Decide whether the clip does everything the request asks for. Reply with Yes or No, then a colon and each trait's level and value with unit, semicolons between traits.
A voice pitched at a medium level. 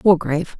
Yes: medium, 165 Hz